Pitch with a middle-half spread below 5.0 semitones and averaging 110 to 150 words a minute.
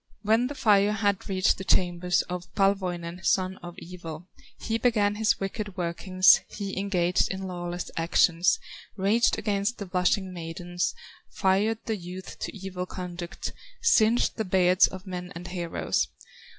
Yes: narrow, 2.4 semitones; average, 145 wpm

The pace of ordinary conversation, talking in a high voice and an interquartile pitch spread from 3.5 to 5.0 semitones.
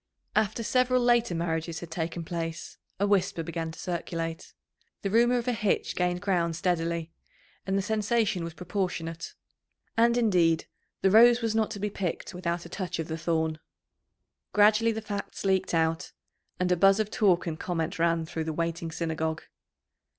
No: average, 170 wpm; medium, 180 Hz; average, 4.1 semitones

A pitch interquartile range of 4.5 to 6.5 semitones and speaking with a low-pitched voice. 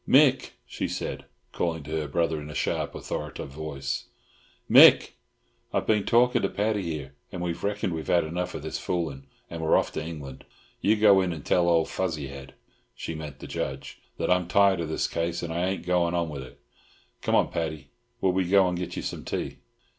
No: average, 3.3 semitones; very low, 85 Hz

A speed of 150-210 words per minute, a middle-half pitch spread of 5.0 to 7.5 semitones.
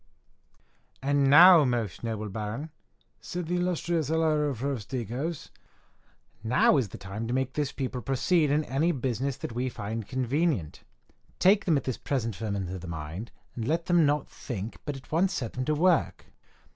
Yes: average, 170 wpm; wide, 5.4 semitones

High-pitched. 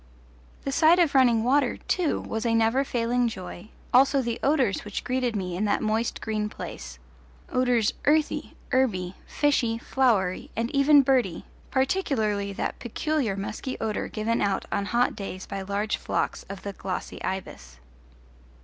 Yes: high, 230 Hz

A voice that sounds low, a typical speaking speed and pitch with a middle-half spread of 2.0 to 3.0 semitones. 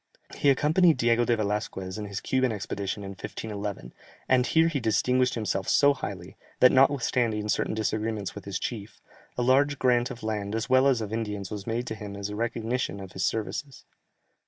No: low, 110 Hz; average, 185 wpm; average, 3.8 semitones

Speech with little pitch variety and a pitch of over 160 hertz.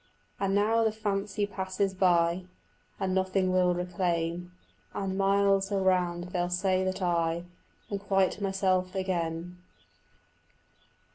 Yes: narrow, 1.7 semitones; medium, 185 Hz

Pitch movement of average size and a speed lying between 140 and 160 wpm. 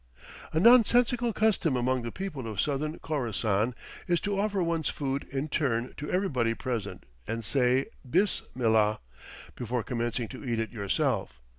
No: wide, 6.5 semitones; average, 150 wpm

